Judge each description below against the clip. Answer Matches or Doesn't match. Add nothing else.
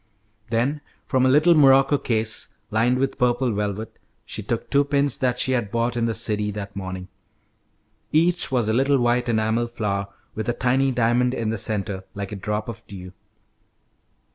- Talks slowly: Doesn't match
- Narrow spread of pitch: Doesn't match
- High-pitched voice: Doesn't match